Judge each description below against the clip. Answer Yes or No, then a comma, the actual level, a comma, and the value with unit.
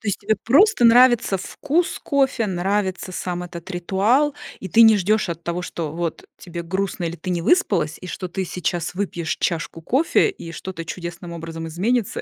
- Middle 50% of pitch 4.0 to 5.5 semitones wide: Yes, average, 4.5 semitones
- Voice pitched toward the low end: No, medium, 185 Hz